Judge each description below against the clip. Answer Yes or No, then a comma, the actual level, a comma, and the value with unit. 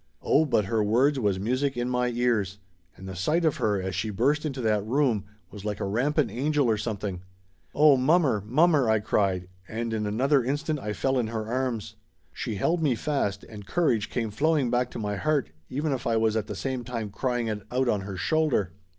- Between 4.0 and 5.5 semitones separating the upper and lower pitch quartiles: Yes, average, 4.9 semitones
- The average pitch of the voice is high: No, low, 120 Hz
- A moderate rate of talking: No, fast, 210 wpm